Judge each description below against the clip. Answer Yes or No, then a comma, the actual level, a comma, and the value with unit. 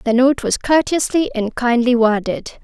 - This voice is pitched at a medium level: No, very high, 250 Hz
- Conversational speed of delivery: Yes, average, 160 wpm